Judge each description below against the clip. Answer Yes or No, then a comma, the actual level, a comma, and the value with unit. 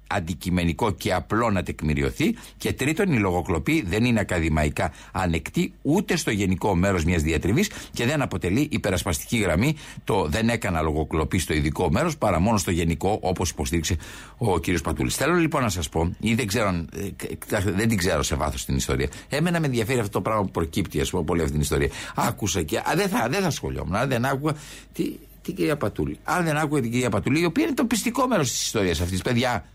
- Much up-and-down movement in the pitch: Yes, wide, 6.6 semitones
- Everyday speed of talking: No, fast, 190 wpm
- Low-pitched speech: Yes, low, 100 Hz